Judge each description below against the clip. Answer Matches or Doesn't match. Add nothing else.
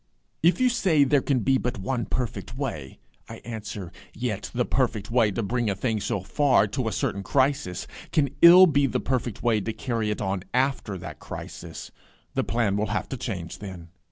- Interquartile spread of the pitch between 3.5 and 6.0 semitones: Matches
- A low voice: Matches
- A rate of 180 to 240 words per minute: Matches